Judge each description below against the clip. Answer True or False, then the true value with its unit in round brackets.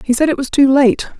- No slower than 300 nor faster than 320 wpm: True (305 wpm)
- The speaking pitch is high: True (270 Hz)